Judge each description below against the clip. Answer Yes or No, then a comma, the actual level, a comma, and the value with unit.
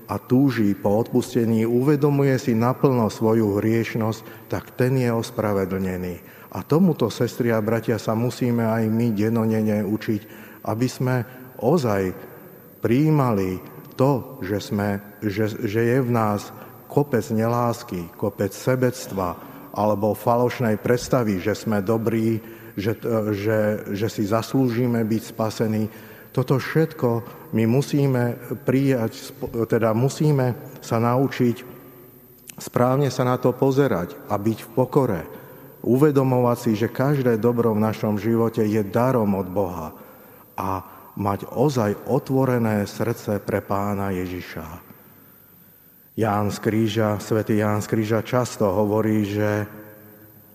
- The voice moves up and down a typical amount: Yes, average, 3.0 semitones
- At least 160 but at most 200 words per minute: No, average, 120 wpm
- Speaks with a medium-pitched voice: No, low, 115 Hz